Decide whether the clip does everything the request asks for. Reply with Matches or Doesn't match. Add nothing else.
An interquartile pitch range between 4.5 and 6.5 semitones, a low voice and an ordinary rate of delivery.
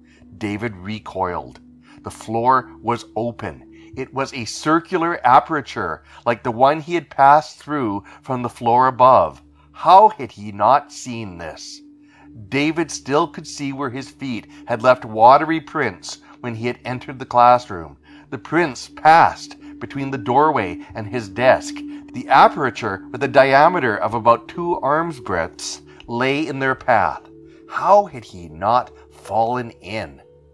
Matches